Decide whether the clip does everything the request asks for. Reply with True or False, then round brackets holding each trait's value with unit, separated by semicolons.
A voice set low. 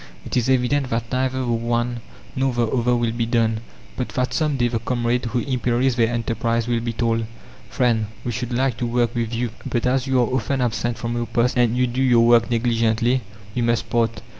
True (120 Hz)